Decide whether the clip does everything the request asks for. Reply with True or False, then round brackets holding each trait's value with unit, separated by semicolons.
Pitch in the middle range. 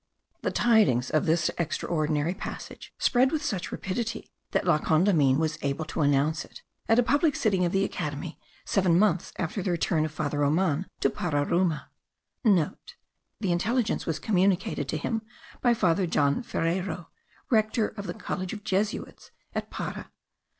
True (175 Hz)